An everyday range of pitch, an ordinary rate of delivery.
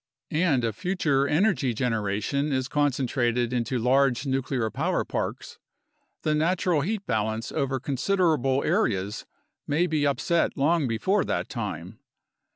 No: average, 4.4 semitones; slow, 125 wpm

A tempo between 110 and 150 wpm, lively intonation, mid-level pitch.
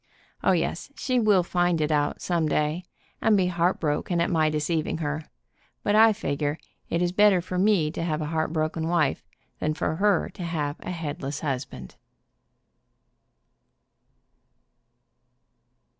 No: average, 140 wpm; average, 3.0 semitones; medium, 165 Hz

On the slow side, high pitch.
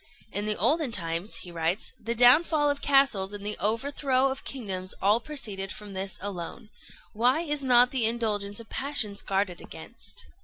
No: average, 165 wpm; high, 220 Hz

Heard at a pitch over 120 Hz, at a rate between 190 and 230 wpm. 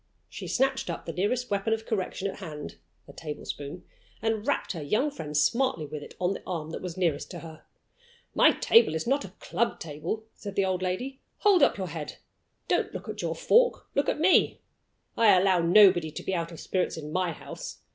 Yes: medium, 185 Hz; fast, 205 wpm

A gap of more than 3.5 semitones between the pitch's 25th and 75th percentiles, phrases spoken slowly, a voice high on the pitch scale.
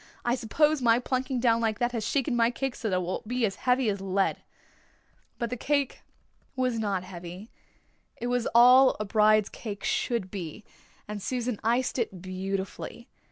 No: average, 3.9 semitones; average, 175 wpm; high, 230 Hz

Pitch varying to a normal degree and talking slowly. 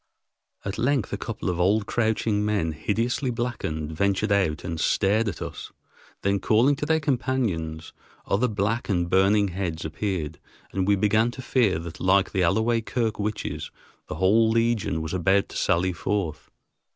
No: average, 3.9 semitones; average, 165 wpm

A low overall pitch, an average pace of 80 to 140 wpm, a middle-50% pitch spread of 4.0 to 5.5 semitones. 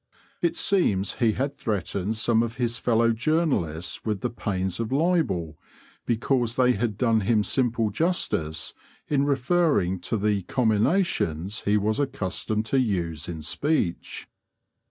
Yes: low, 110 Hz; slow, 135 wpm; average, 5.2 semitones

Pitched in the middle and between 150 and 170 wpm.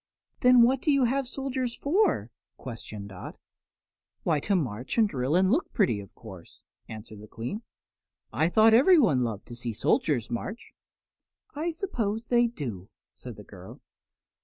Yes: medium, 175 Hz; average, 155 wpm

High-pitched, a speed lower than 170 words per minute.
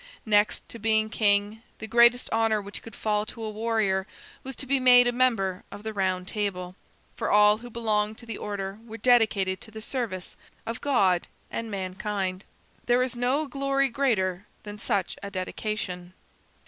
No: high, 215 Hz; average, 175 wpm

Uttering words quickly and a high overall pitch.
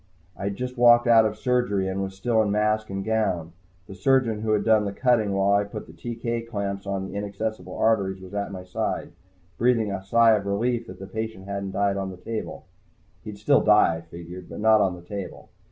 No: fast, 220 wpm; low, 100 Hz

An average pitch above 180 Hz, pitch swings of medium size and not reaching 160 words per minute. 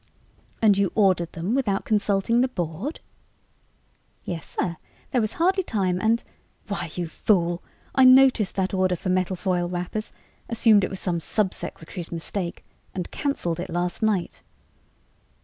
Yes: high, 190 Hz; average, 3.8 semitones; average, 150 wpm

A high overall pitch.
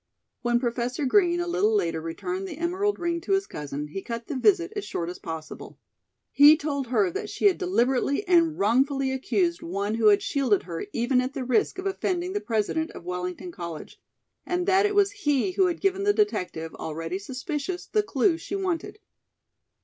Yes: very high, 275 Hz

